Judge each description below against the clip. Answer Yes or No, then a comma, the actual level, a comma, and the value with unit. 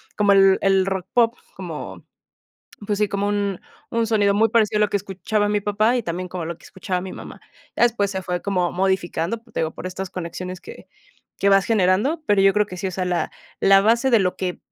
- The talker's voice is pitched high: Yes, high, 195 Hz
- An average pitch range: No, narrow, 2.3 semitones